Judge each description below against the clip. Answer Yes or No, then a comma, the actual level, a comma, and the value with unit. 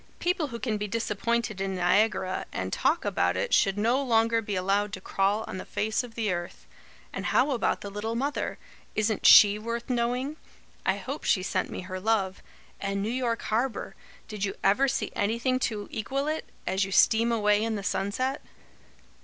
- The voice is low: No, high, 215 Hz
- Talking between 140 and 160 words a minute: No, average, 185 wpm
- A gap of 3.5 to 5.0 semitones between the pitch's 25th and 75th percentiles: No, average, 3.1 semitones